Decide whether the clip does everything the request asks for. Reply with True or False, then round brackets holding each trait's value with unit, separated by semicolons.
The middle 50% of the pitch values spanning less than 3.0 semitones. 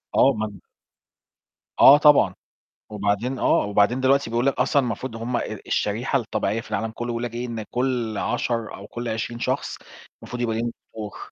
True (2.4 semitones)